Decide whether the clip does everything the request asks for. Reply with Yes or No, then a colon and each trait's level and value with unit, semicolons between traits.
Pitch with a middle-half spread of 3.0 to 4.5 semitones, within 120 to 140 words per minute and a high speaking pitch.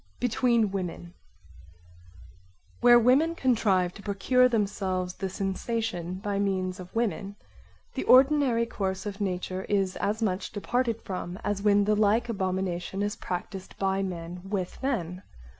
Yes: average, 3.6 semitones; slow, 135 wpm; high, 200 Hz